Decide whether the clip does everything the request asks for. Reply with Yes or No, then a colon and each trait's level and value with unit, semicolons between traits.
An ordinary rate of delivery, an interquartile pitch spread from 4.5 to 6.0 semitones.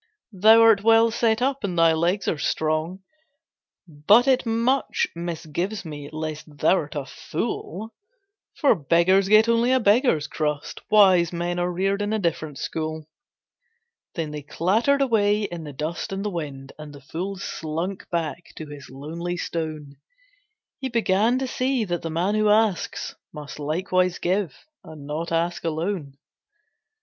Yes: average, 155 wpm; average, 5.2 semitones